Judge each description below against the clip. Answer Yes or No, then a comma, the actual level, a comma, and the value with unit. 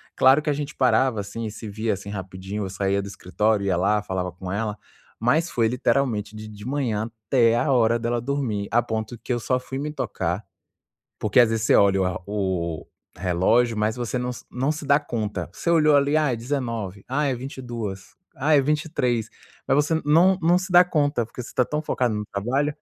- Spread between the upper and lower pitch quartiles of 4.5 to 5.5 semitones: Yes, average, 5.1 semitones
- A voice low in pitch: Yes, low, 120 Hz